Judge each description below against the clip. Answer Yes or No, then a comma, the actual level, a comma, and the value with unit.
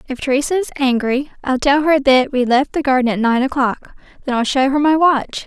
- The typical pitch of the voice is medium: No, very high, 270 Hz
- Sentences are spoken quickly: Yes, fast, 230 wpm